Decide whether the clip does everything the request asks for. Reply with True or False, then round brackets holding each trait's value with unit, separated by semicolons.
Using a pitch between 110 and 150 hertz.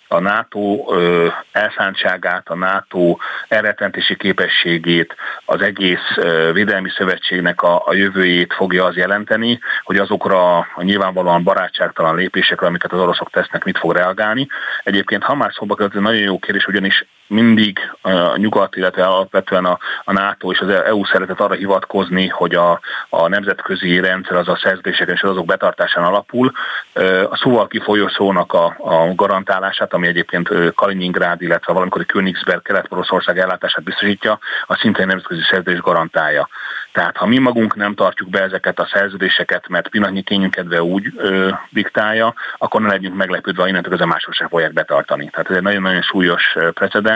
False (95 Hz)